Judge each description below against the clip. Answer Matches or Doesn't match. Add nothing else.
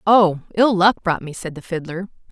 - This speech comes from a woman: Matches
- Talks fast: Matches